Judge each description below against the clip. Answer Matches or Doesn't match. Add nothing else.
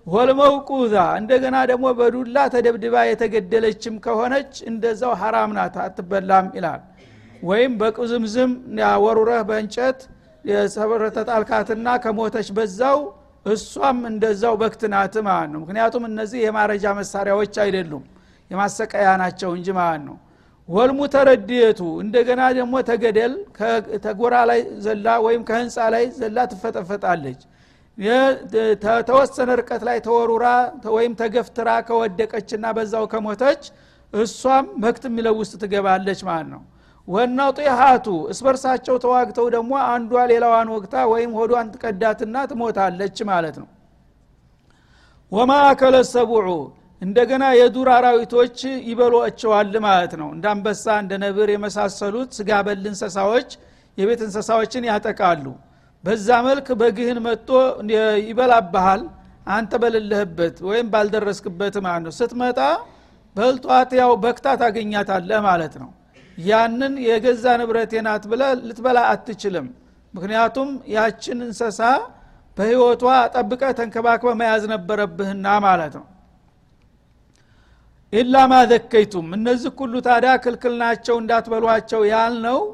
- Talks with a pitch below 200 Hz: Doesn't match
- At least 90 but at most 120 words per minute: Matches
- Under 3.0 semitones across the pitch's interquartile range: Matches